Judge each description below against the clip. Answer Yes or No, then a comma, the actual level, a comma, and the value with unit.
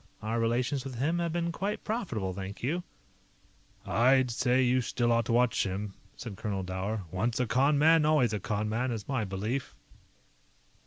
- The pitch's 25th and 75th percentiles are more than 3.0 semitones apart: Yes, average, 4.3 semitones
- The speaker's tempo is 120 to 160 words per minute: No, average, 175 wpm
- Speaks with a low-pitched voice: Yes, low, 120 Hz